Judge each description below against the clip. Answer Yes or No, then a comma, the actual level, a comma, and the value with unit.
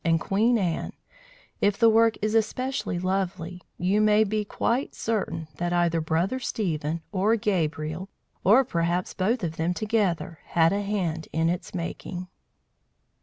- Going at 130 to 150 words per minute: Yes, average, 145 wpm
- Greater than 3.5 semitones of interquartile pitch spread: Yes, average, 4.2 semitones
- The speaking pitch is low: No, medium, 185 Hz